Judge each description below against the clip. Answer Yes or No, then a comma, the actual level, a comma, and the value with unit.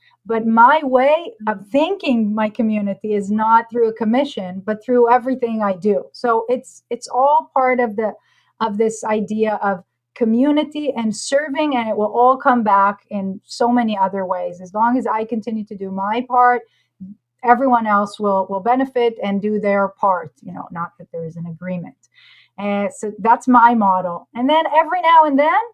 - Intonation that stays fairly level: No, average, 4.0 semitones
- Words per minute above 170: Yes, average, 185 wpm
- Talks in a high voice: Yes, high, 225 Hz